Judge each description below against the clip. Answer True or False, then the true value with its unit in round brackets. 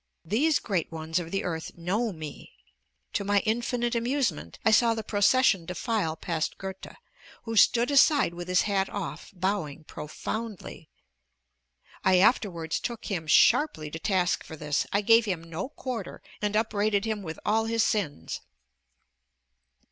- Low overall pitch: False (200 Hz)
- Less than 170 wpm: True (150 wpm)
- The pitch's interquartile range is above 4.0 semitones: True (5.2 semitones)